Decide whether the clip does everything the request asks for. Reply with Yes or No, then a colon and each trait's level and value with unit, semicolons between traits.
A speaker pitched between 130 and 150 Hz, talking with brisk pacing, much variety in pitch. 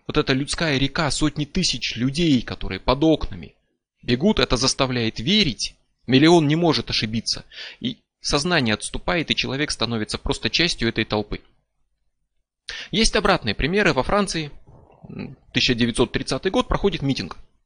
No: low, 135 Hz; average, 125 wpm; wide, 6.1 semitones